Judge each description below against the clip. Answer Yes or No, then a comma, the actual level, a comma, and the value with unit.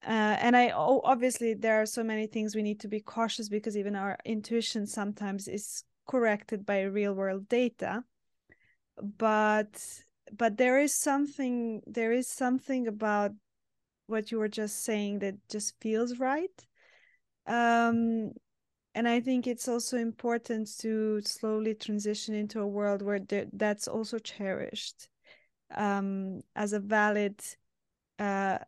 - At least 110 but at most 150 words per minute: Yes, average, 140 wpm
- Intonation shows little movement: Yes, narrow, 2.1 semitones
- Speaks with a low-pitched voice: No, high, 220 Hz